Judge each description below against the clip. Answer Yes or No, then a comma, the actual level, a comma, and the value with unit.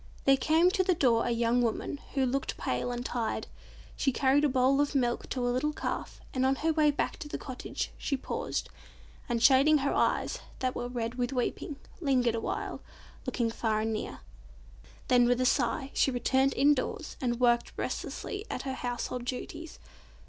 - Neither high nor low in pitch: No, very high, 255 Hz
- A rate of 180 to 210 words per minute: Yes, average, 185 wpm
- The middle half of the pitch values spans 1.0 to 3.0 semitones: Yes, narrow, 2.5 semitones